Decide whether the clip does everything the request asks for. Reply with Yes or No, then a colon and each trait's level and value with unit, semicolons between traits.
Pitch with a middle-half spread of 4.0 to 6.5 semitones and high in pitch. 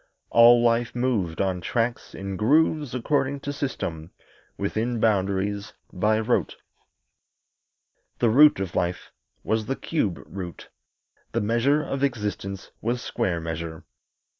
No: average, 4.4 semitones; low, 110 Hz